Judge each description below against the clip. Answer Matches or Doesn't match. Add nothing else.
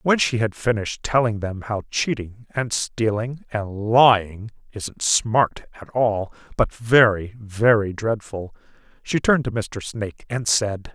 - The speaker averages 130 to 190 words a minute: Matches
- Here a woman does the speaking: Doesn't match